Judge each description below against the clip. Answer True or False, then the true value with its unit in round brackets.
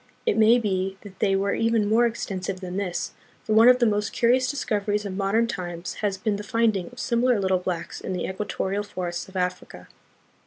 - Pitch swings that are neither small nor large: True (3.3 semitones)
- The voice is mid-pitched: False (205 Hz)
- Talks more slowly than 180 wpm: False (205 wpm)